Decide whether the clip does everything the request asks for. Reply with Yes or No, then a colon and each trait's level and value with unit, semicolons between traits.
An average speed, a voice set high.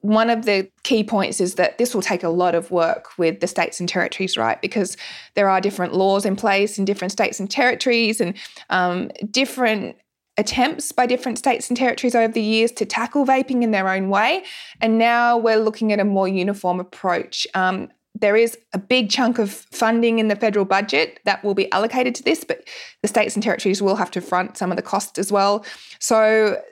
No: fast, 210 wpm; high, 215 Hz